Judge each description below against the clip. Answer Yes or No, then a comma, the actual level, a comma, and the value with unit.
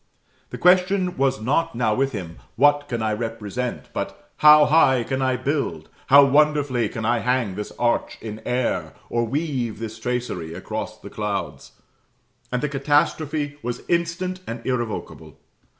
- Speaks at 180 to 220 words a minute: No, average, 150 wpm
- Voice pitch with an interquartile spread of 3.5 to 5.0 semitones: Yes, average, 4.3 semitones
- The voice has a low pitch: Yes, low, 130 Hz